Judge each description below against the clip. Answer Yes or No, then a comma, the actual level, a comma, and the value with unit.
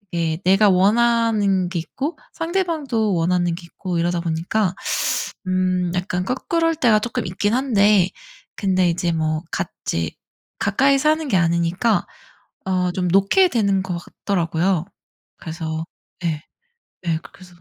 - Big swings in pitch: No, average, 4.5 semitones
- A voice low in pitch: No, medium, 185 Hz